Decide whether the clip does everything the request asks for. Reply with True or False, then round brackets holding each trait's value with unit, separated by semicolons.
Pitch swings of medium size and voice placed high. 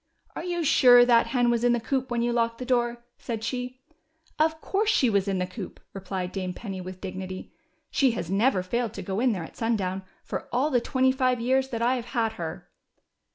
True (4.6 semitones; 235 Hz)